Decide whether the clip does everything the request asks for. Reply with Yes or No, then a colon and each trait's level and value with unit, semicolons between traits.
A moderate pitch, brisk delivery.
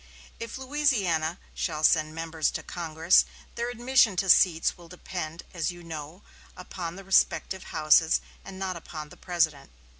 No: medium, 175 Hz; average, 150 wpm